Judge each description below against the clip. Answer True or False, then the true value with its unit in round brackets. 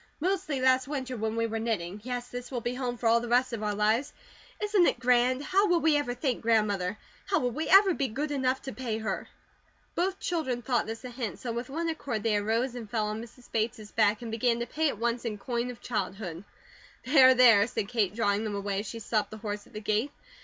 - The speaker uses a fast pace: True (240 wpm)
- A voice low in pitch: False (240 Hz)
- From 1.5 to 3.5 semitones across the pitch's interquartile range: True (3.2 semitones)